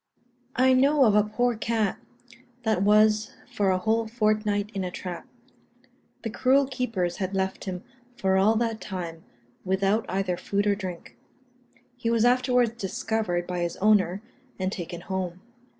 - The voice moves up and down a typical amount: Yes, average, 3.3 semitones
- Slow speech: No, average, 150 wpm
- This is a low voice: No, high, 205 Hz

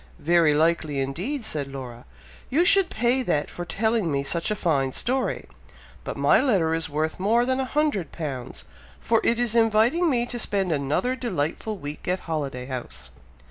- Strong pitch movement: Yes, wide, 8.4 semitones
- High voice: No, medium, 175 Hz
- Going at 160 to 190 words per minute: Yes, average, 175 wpm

